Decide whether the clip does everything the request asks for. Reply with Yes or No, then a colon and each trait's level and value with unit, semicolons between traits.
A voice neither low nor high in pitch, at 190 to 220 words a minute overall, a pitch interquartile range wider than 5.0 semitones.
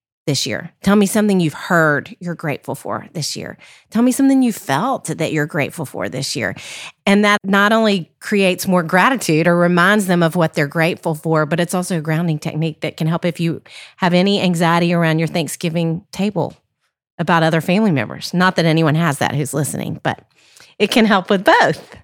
No: medium, 170 Hz; average, 200 wpm; average, 3.2 semitones